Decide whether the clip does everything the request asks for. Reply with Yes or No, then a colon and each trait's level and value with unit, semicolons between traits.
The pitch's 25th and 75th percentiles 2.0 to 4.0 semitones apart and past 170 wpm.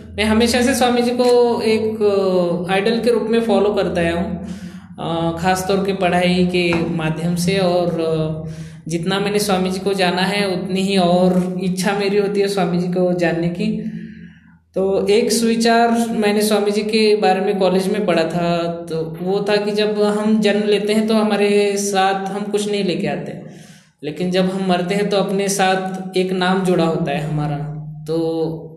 Yes: narrow, 2.6 semitones; average, 180 wpm